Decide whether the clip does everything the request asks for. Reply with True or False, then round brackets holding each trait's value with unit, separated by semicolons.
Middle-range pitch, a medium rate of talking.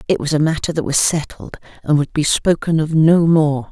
False (155 Hz; 225 wpm)